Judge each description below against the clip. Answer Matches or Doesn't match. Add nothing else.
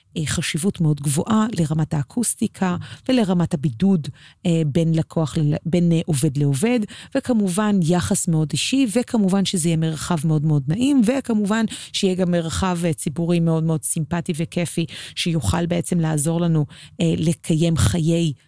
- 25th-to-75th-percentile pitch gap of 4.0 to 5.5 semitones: Doesn't match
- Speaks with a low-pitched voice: Doesn't match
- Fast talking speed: Doesn't match